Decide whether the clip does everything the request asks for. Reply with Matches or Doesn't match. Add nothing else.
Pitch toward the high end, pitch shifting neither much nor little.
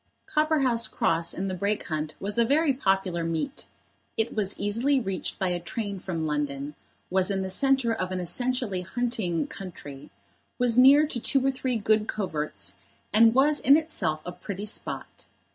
Doesn't match